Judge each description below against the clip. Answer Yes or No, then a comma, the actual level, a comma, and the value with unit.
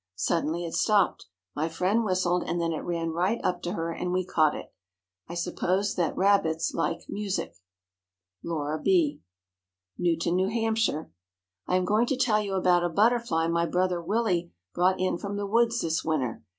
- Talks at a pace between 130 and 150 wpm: No, average, 175 wpm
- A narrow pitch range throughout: No, average, 3.5 semitones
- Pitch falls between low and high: Yes, medium, 180 Hz